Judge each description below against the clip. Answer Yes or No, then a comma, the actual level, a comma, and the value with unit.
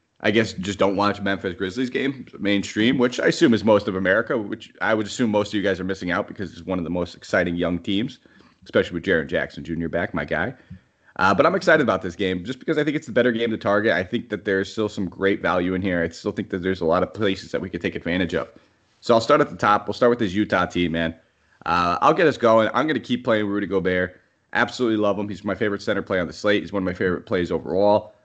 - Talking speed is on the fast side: Yes, fast, 275 wpm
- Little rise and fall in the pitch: No, average, 3.2 semitones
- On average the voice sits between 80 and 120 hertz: Yes, low, 100 Hz